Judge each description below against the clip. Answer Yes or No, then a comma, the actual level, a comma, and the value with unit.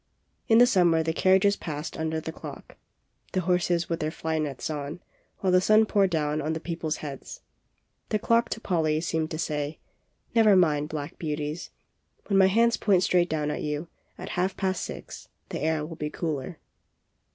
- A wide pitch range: No, average, 3.5 semitones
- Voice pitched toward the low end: No, medium, 165 Hz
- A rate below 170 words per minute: No, average, 185 wpm